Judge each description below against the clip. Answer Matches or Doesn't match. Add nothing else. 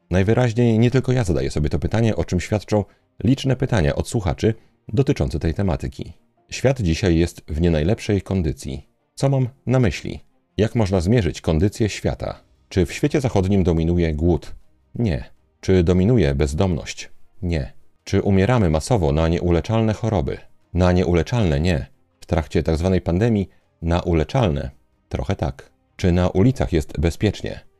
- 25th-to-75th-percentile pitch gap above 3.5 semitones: Matches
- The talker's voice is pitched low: Matches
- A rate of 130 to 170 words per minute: Matches